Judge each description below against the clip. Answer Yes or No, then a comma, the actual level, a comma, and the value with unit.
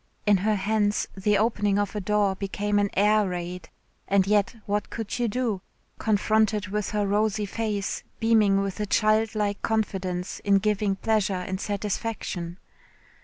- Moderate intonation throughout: No, narrow, 1.5 semitones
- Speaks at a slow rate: No, average, 155 wpm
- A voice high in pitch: Yes, high, 205 Hz